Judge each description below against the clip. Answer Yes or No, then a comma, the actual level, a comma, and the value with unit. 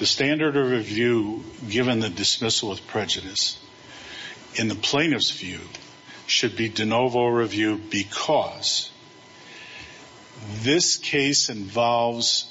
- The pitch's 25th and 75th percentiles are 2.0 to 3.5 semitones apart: Yes, average, 2.7 semitones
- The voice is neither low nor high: No, low, 115 Hz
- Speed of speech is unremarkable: No, slow, 105 wpm